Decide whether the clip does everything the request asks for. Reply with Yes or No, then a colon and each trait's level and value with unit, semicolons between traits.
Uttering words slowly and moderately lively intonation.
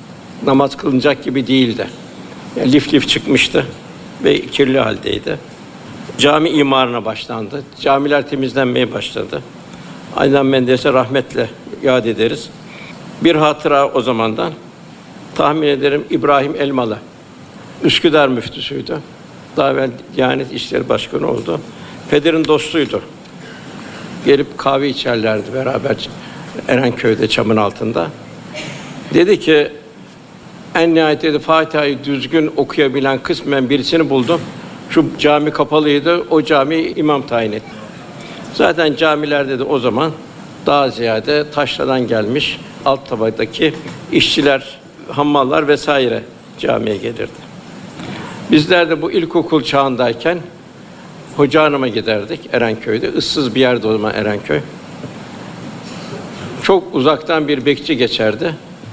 No: average, 105 wpm; average, 3.1 semitones